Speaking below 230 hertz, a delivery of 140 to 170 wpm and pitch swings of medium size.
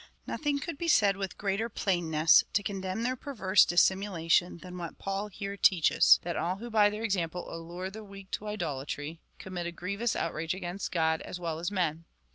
No: high, 190 Hz; average, 195 wpm; average, 3.2 semitones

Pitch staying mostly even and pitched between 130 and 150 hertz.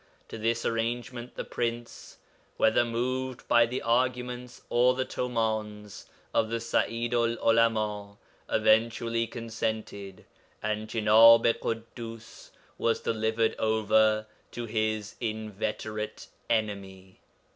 No: narrow, 1.5 semitones; low, 115 Hz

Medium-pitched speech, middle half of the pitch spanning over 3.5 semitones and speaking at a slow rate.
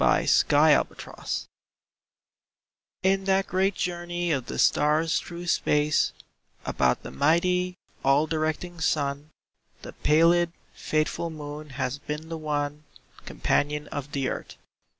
No: medium, 155 Hz; average, 2.9 semitones; slow, 120 wpm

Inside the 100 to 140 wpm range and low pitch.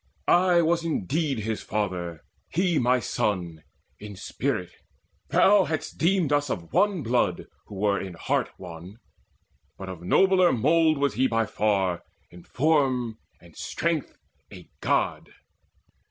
Yes: slow, 135 wpm; low, 125 Hz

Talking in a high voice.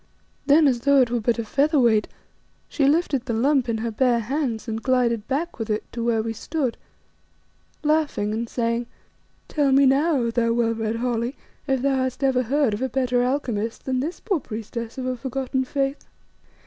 Yes: very high, 250 Hz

